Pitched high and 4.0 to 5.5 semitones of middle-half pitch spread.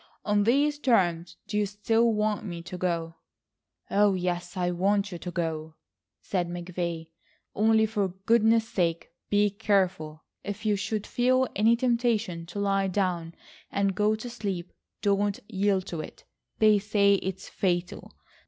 No: high, 200 Hz; average, 3.3 semitones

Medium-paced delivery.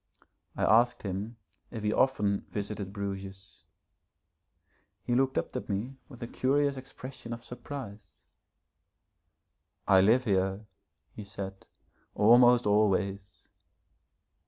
No: slow, 110 wpm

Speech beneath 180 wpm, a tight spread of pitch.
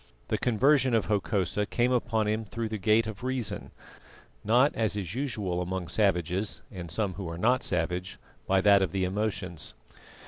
No: average, 170 wpm; average, 3.6 semitones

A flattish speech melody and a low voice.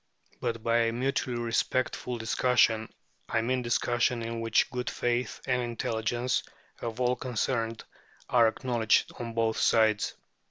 Yes: narrow, 1.5 semitones; low, 120 Hz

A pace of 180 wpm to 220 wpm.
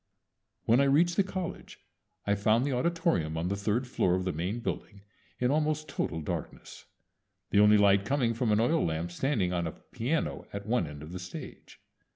Yes: average, 190 wpm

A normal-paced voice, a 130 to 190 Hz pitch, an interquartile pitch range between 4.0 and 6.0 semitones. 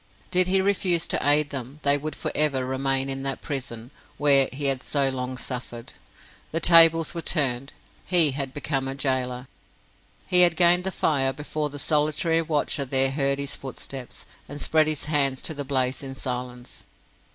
No: average, 175 wpm; medium, 140 Hz; average, 2.7 semitones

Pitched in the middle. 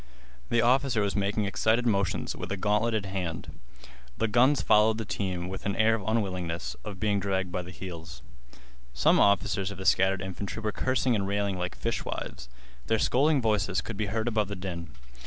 No: low, 100 Hz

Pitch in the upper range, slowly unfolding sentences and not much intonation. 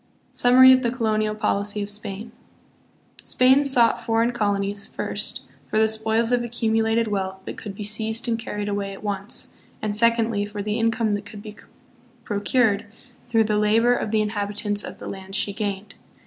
No: high, 215 Hz; average, 175 wpm; narrow, 2.0 semitones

